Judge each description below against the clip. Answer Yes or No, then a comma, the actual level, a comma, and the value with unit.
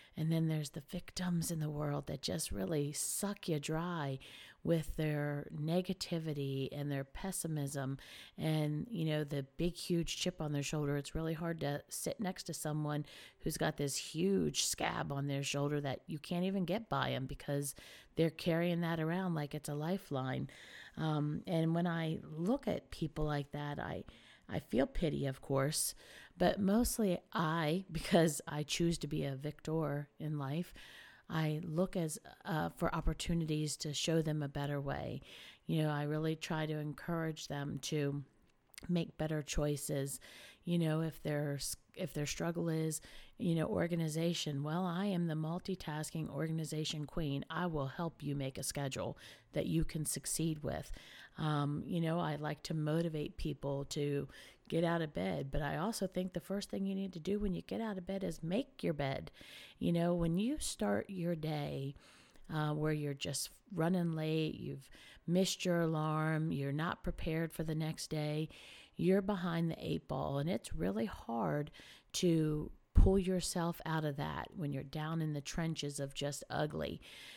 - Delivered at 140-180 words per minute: Yes, average, 175 wpm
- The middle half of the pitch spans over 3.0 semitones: No, average, 2.7 semitones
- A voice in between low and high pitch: Yes, medium, 155 Hz